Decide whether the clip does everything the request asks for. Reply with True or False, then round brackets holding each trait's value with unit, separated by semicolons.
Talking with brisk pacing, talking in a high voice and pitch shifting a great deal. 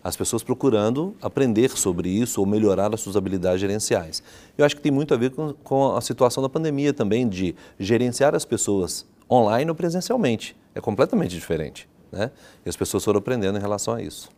False (190 wpm; 115 Hz; 5.8 semitones)